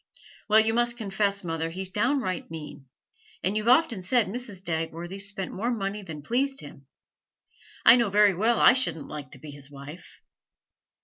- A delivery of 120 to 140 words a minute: No, average, 175 wpm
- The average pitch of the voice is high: Yes, high, 195 Hz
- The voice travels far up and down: Yes, wide, 5.9 semitones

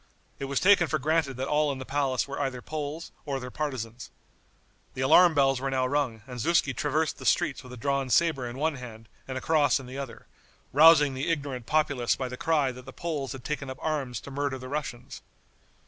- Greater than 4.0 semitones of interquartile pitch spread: No, average, 2.8 semitones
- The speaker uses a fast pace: Yes, fast, 220 wpm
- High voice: No, low, 135 Hz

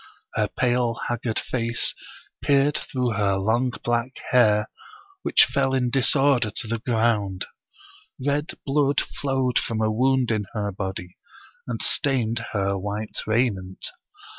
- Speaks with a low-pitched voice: Yes, low, 115 Hz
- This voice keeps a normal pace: No, slow, 130 wpm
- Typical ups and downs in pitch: Yes, average, 3.6 semitones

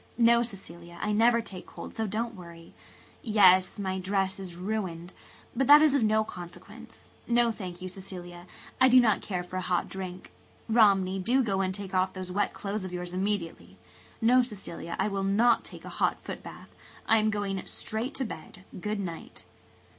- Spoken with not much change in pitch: No, average, 3.2 semitones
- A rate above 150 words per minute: Yes, average, 185 wpm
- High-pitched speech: Yes, high, 195 Hz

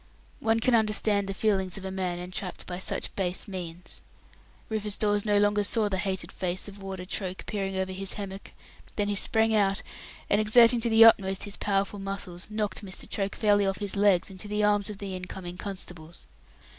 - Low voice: No, high, 200 Hz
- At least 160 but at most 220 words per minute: Yes, average, 195 wpm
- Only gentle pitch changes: Yes, narrow, 1.8 semitones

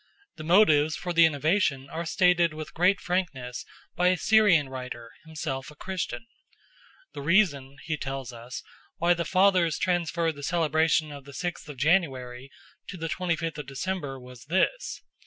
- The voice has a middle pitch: Yes, medium, 160 Hz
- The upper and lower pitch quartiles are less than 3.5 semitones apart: No, average, 4.5 semitones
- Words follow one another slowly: No, average, 160 wpm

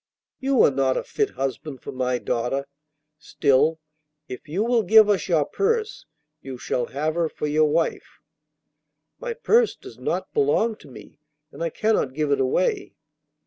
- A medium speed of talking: Yes, average, 165 wpm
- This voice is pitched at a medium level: Yes, medium, 155 Hz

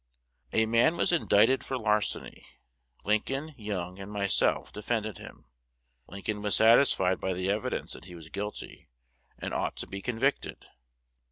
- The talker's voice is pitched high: No, low, 105 Hz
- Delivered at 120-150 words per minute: Yes, average, 145 wpm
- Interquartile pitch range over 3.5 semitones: No, average, 3.0 semitones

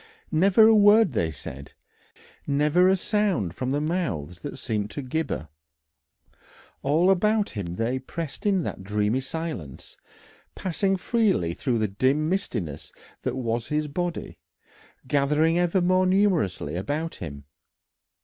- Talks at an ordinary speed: No, slow, 130 wpm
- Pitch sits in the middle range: Yes, medium, 150 Hz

